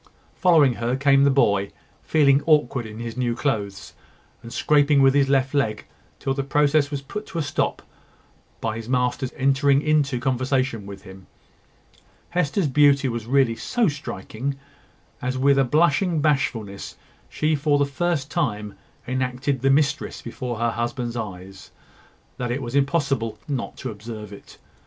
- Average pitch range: Yes, average, 3.4 semitones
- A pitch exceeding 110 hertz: Yes, low, 135 Hz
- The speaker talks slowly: No, average, 155 wpm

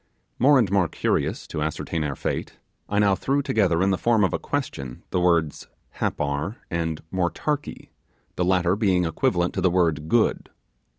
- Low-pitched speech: Yes, very low, 90 Hz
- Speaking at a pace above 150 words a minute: Yes, average, 170 wpm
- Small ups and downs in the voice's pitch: No, average, 3.8 semitones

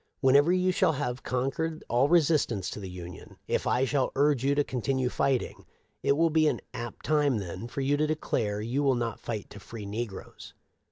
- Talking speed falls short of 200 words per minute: No, fast, 205 wpm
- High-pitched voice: No, low, 130 Hz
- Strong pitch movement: No, average, 4.1 semitones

